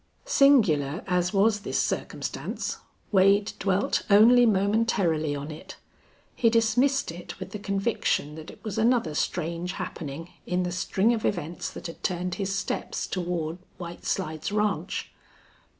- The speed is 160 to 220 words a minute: No, average, 140 wpm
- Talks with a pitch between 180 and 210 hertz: Yes, high, 190 Hz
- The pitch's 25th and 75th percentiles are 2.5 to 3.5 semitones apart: No, average, 4.1 semitones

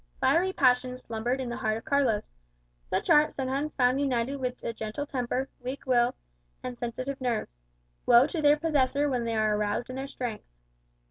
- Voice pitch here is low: No, very high, 255 Hz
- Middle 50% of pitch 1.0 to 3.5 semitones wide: Yes, average, 2.7 semitones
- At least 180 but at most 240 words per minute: Yes, average, 185 wpm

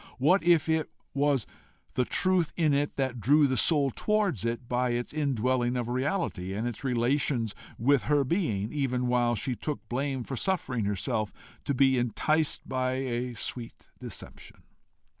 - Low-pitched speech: Yes, low, 130 Hz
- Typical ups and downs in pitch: Yes, average, 3.4 semitones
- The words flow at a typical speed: Yes, average, 155 wpm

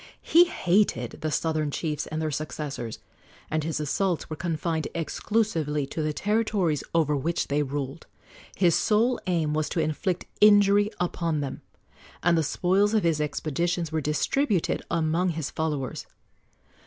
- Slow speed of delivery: No, average, 145 wpm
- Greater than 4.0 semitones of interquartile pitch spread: No, average, 3.3 semitones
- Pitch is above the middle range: No, medium, 160 Hz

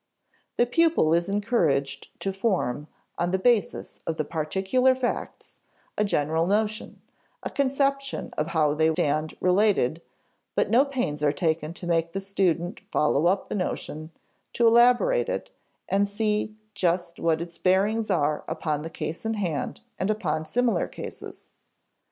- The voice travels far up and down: Yes, wide, 5.7 semitones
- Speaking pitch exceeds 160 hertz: Yes, medium, 185 Hz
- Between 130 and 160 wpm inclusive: Yes, average, 150 wpm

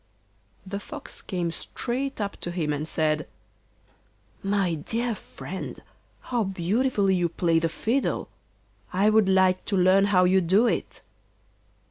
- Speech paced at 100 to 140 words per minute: Yes, slow, 135 wpm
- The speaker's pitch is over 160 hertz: Yes, high, 190 Hz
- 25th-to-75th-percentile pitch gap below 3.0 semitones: No, average, 3.7 semitones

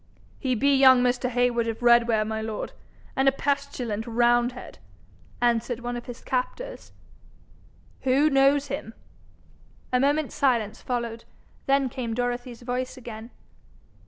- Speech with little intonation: Yes, narrow, 2.2 semitones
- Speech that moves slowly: Yes, slow, 130 wpm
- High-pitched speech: Yes, high, 245 Hz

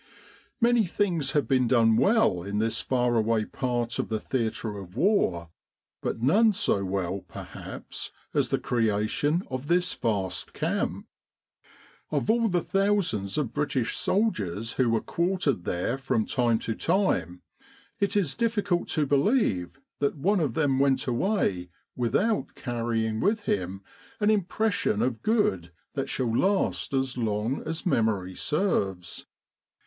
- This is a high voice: No, low, 130 Hz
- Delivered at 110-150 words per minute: Yes, average, 145 wpm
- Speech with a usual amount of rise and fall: No, wide, 9.0 semitones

